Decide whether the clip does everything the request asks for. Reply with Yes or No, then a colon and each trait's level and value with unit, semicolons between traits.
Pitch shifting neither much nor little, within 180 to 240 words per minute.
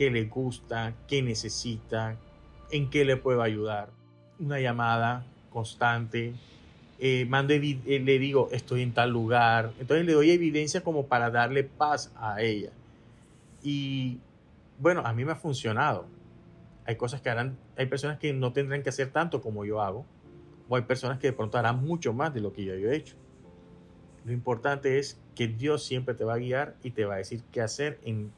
Yes: average, 3.5 semitones; average, 185 wpm